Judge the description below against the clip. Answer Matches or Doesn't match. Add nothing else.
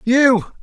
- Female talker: Doesn't match